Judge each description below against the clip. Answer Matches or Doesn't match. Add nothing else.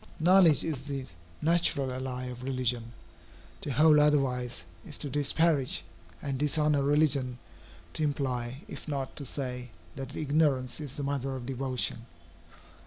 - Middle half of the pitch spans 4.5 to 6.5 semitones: Doesn't match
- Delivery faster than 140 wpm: Doesn't match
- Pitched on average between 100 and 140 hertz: Matches